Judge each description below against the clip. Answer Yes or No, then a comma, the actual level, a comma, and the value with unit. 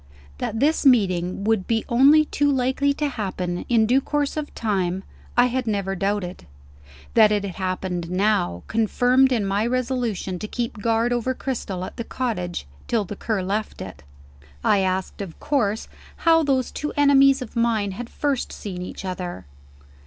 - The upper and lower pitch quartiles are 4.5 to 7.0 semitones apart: Yes, average, 5.2 semitones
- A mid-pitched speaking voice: No, high, 220 Hz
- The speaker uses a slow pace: No, average, 170 wpm